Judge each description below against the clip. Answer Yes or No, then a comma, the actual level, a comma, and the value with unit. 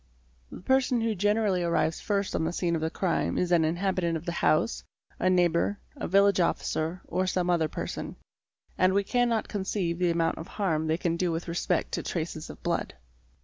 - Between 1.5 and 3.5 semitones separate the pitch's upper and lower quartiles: Yes, average, 3.0 semitones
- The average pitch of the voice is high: No, medium, 175 Hz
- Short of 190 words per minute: No, average, 195 wpm